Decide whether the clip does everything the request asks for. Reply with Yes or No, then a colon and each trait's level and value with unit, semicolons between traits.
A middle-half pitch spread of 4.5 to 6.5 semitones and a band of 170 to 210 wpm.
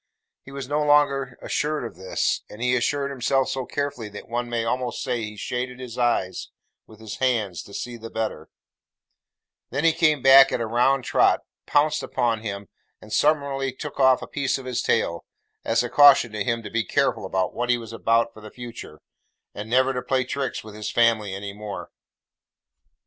No: average, 3.4 semitones; average, 190 wpm